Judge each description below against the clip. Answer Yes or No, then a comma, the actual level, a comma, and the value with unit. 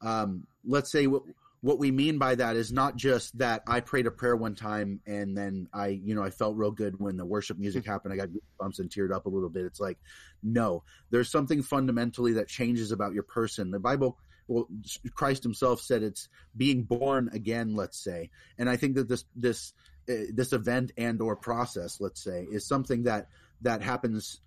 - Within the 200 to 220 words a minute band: Yes, fast, 205 wpm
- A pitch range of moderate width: Yes, average, 3.7 semitones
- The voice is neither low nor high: No, low, 115 Hz